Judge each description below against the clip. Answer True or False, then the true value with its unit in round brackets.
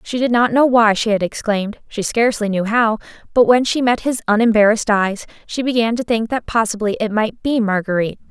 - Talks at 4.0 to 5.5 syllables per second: False (5.8 syllables/s)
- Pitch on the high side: True (225 Hz)